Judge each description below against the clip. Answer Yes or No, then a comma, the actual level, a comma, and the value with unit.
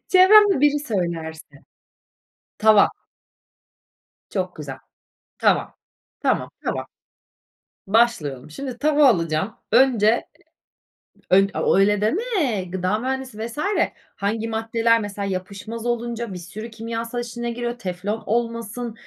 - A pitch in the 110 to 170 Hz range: No, high, 225 Hz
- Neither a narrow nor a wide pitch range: Yes, average, 3.5 semitones